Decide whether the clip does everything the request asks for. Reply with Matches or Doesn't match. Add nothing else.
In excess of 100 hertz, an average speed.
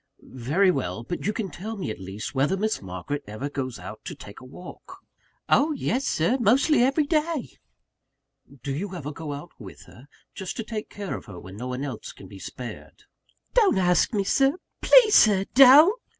Matches